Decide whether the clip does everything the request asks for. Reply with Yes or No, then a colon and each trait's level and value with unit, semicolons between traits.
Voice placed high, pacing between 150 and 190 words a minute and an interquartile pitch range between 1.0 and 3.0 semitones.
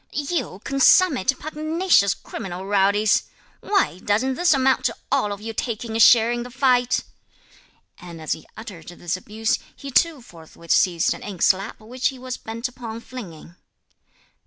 No: high, 230 Hz; average, 155 wpm; average, 5.2 semitones